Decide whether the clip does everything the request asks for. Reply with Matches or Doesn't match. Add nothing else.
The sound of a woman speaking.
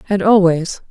Matches